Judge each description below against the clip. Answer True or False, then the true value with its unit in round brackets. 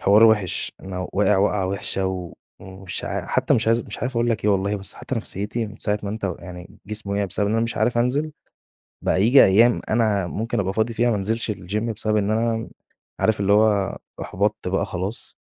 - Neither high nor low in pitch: False (105 Hz)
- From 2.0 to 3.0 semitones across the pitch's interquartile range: True (2.7 semitones)